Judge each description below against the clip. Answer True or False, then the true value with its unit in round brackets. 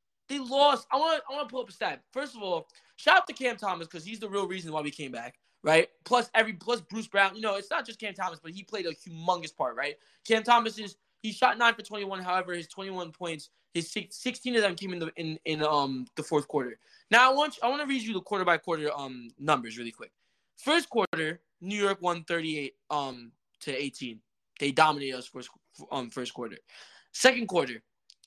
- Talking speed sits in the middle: False (225 wpm)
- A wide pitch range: True (6.7 semitones)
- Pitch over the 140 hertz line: True (185 Hz)